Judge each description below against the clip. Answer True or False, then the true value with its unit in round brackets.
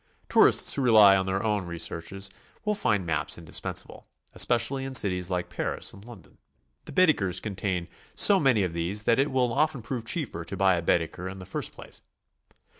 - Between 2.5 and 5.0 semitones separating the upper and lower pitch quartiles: False (5.4 semitones)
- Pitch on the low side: True (100 Hz)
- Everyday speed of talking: True (190 wpm)